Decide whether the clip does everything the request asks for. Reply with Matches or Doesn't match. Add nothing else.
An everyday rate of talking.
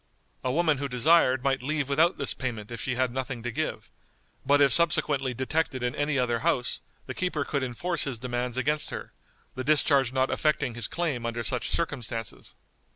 Matches